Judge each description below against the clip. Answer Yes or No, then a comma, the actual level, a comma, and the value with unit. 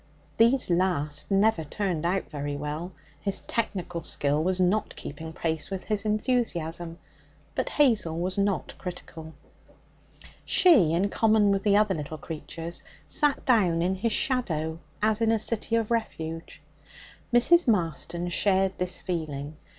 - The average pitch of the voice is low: No, medium, 185 Hz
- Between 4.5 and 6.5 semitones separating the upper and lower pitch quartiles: Yes, average, 4.9 semitones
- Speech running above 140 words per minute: No, slow, 135 wpm